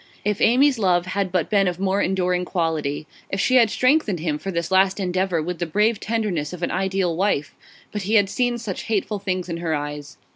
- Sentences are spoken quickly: Yes, fast, 215 wpm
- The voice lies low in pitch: No, high, 190 Hz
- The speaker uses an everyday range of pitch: Yes, average, 3.2 semitones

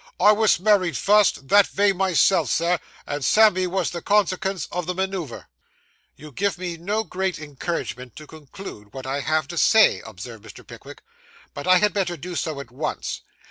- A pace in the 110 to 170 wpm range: No, average, 180 wpm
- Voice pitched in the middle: Yes, medium, 175 Hz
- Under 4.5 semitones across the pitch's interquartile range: No, average, 4.9 semitones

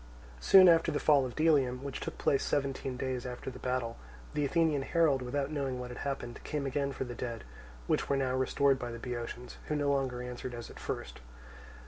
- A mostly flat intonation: Yes, narrow, 2.3 semitones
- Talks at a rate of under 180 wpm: No, fast, 205 wpm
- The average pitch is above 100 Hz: Yes, low, 135 Hz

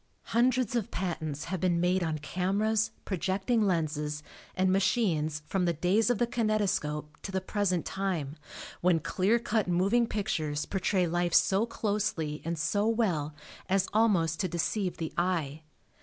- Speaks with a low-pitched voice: No, medium, 185 Hz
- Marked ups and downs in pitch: No, average, 4.3 semitones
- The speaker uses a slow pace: No, average, 150 wpm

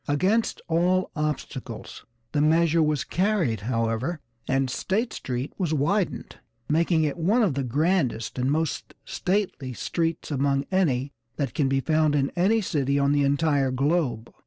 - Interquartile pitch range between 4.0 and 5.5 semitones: Yes, average, 4.3 semitones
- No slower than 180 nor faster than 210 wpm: No, average, 150 wpm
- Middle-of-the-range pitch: Yes, medium, 150 Hz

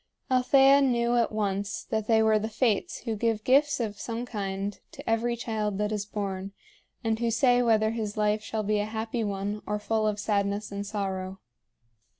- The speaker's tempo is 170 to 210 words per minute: Yes, average, 185 wpm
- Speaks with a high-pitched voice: Yes, high, 215 Hz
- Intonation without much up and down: Yes, narrow, 2.3 semitones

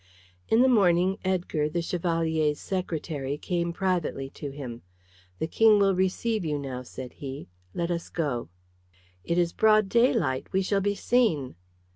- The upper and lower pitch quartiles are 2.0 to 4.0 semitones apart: No, average, 4.7 semitones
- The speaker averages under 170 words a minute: Yes, average, 150 wpm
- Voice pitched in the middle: Yes, medium, 170 Hz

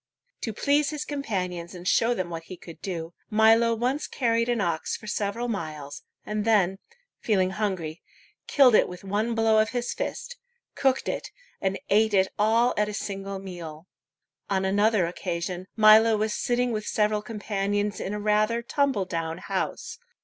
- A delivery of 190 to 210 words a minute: No, average, 165 wpm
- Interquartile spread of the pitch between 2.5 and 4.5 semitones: Yes, average, 3.5 semitones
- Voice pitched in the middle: No, high, 210 Hz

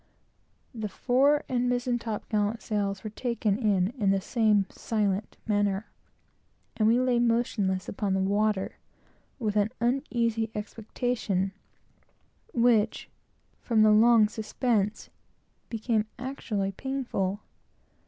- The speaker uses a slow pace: Yes, slow, 115 wpm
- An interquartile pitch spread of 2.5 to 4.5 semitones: Yes, average, 2.8 semitones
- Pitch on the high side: Yes, high, 215 Hz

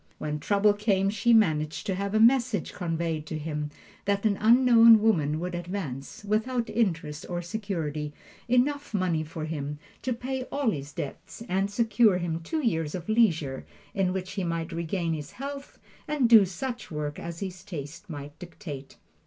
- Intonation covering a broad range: Yes, wide, 5.7 semitones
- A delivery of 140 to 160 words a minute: No, average, 170 wpm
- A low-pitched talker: No, medium, 185 Hz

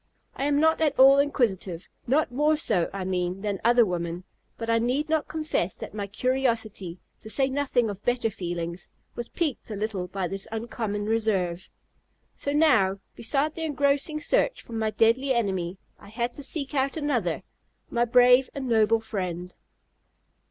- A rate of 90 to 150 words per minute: No, average, 165 wpm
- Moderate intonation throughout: No, wide, 6.0 semitones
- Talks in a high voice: Yes, high, 230 Hz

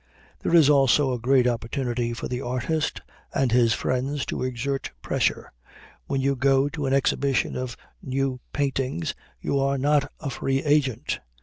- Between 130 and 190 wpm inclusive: Yes, average, 160 wpm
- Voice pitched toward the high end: No, low, 135 Hz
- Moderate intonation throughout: No, narrow, 1.9 semitones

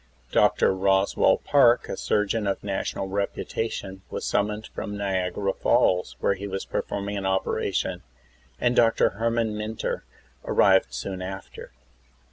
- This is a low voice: Yes, low, 100 Hz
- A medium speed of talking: No, slow, 130 wpm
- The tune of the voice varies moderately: No, narrow, 1.9 semitones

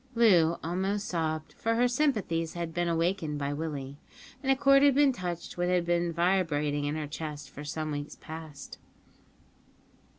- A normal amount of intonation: Yes, average, 4.1 semitones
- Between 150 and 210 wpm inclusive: Yes, average, 165 wpm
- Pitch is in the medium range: Yes, medium, 170 Hz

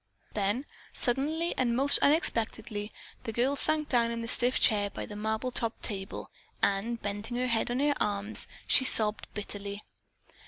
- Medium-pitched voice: No, high, 230 Hz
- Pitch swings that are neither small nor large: Yes, average, 3.5 semitones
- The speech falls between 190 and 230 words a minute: No, average, 160 wpm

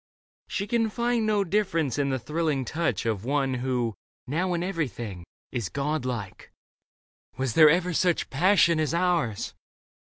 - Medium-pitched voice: Yes, medium, 155 Hz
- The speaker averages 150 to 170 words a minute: Yes, average, 155 wpm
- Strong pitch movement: Yes, wide, 5.9 semitones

